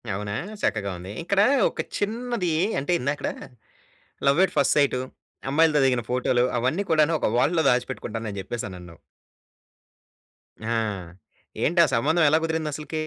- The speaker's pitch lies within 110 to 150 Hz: Yes, medium, 140 Hz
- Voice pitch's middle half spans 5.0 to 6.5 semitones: Yes, wide, 5.5 semitones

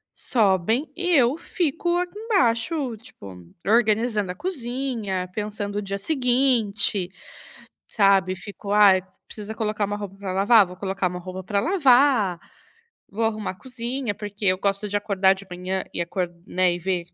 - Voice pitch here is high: Yes, high, 205 Hz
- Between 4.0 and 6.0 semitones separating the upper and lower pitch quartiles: Yes, average, 4.3 semitones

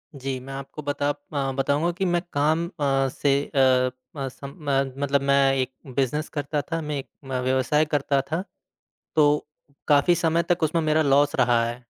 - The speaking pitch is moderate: Yes, medium, 145 Hz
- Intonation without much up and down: Yes, narrow, 2.1 semitones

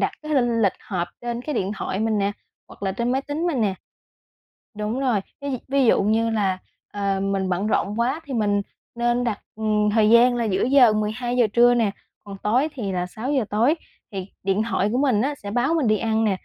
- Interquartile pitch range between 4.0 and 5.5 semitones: No, average, 3.3 semitones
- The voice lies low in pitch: No, high, 225 Hz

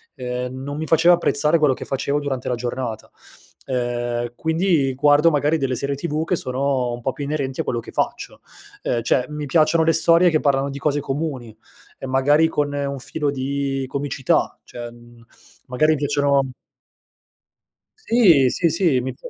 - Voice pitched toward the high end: No, medium, 140 Hz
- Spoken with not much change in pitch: No, average, 3.1 semitones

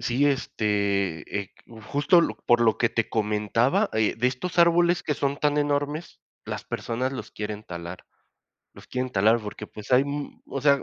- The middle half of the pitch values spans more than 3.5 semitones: Yes, average, 5.2 semitones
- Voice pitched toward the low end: Yes, low, 120 Hz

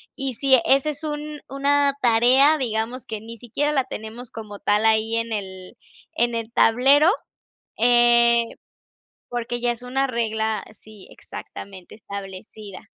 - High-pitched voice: Yes, high, 235 Hz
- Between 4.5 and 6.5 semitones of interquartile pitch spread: No, average, 3.5 semitones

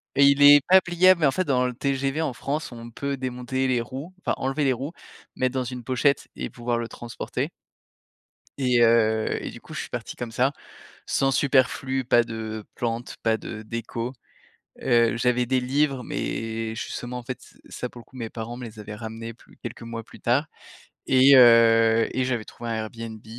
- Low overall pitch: Yes, low, 125 Hz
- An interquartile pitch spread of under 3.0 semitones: Yes, narrow, 2.5 semitones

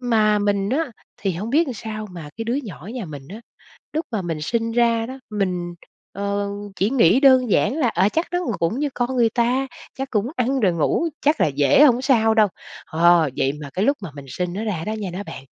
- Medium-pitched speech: No, high, 215 Hz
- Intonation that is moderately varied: No, wide, 5.7 semitones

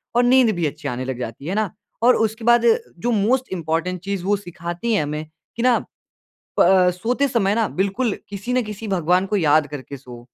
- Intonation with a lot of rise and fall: Yes, wide, 6.4 semitones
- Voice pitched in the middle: No, high, 195 Hz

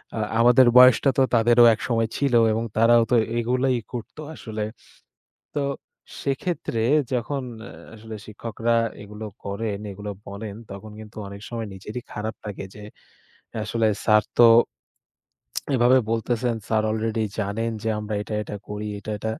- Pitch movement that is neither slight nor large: No, narrow, 2.1 semitones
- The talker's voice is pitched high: No, low, 115 Hz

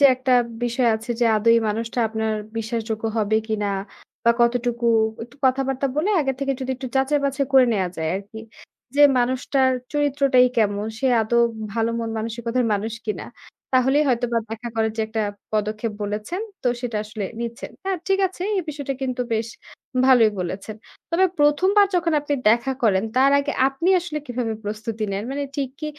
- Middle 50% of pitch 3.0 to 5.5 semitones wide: Yes, average, 3.7 semitones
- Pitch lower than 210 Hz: No, high, 240 Hz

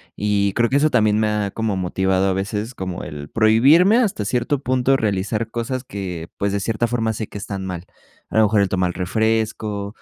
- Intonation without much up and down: No, average, 3.2 semitones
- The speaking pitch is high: No, low, 105 Hz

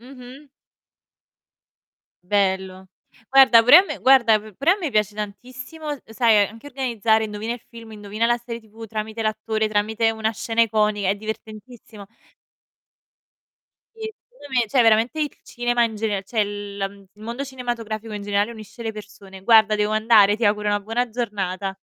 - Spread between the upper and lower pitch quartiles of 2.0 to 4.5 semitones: Yes, narrow, 2.6 semitones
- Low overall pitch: No, high, 220 Hz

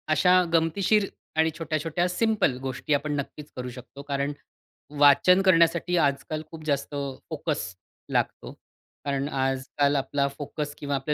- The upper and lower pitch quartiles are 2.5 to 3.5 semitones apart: Yes, average, 2.9 semitones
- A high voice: No, medium, 145 Hz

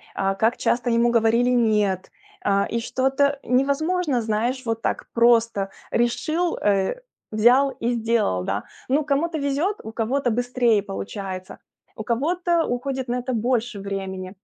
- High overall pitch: Yes, high, 240 Hz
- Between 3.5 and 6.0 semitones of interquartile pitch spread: Yes, average, 3.9 semitones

